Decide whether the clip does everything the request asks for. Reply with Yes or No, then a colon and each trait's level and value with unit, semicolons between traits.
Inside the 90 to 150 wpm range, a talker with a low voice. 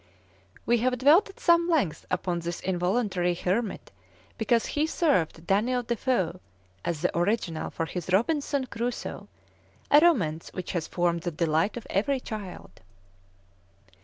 No: average, 140 wpm; high, 200 Hz